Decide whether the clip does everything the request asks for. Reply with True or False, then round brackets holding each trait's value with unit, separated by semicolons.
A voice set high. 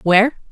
True (215 Hz)